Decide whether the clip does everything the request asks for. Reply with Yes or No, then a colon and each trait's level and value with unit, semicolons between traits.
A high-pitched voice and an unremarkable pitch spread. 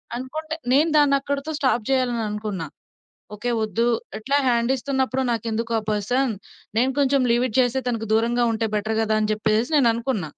Yes: high, 235 Hz; average, 3.3 semitones